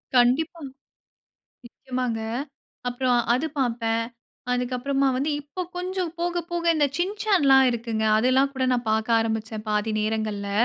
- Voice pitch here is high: Yes, very high, 250 Hz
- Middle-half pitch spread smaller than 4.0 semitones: No, average, 4.5 semitones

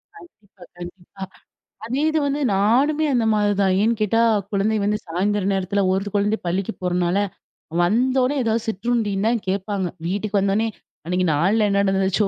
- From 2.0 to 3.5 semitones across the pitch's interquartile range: Yes, average, 2.9 semitones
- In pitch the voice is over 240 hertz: No, high, 205 Hz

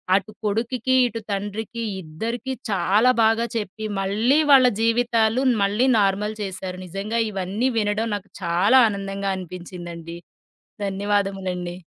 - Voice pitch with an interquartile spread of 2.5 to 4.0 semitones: Yes, average, 3.0 semitones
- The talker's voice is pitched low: No, high, 205 Hz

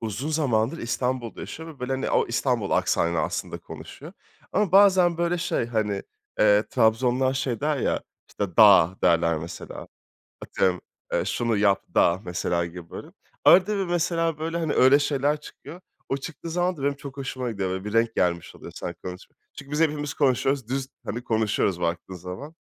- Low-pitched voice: Yes, low, 125 Hz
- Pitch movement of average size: No, wide, 6.9 semitones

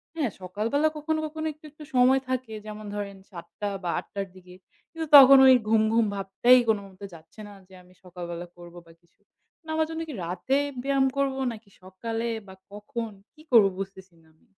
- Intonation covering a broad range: Yes, wide, 6.1 semitones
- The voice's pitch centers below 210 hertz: No, high, 215 Hz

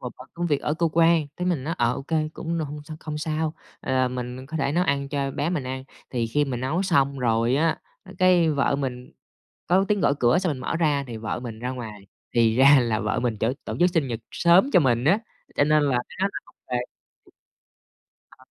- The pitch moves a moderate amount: Yes, average, 4.6 semitones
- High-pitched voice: No, medium, 140 Hz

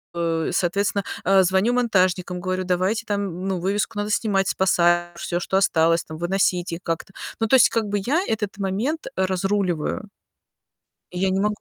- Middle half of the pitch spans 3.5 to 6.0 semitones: No, narrow, 2.6 semitones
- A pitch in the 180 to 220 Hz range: Yes, high, 190 Hz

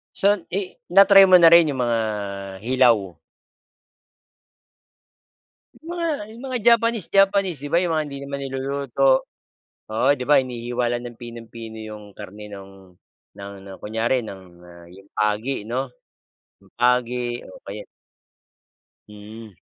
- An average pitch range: No, wide, 5.8 semitones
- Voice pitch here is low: Yes, low, 120 Hz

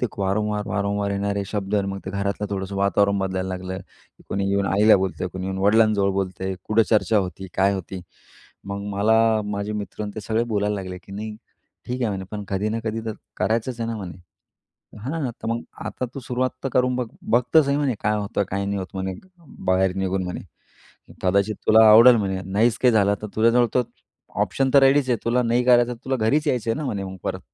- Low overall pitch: Yes, low, 105 Hz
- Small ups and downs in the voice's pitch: No, average, 3.1 semitones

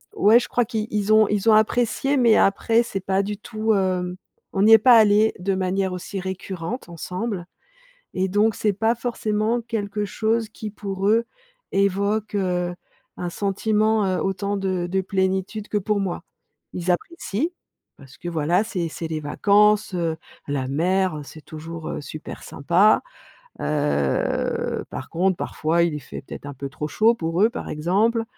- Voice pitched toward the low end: No, high, 195 Hz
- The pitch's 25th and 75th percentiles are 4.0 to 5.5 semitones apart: No, average, 3.5 semitones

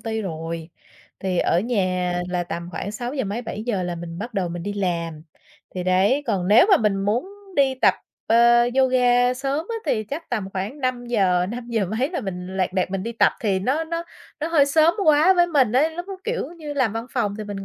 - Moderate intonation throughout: No, wide, 6.2 semitones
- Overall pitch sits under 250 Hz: Yes, high, 220 Hz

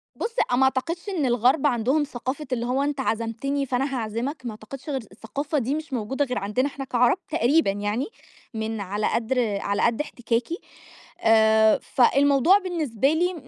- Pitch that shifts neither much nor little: Yes, average, 4.2 semitones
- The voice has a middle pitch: No, very high, 255 Hz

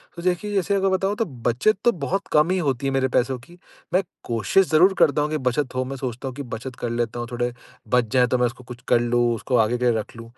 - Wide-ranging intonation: Yes, wide, 6.0 semitones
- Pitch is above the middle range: No, low, 130 Hz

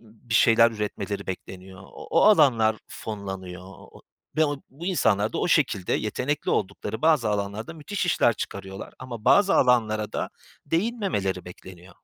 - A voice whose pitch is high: No, low, 110 Hz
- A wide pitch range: Yes, wide, 6.8 semitones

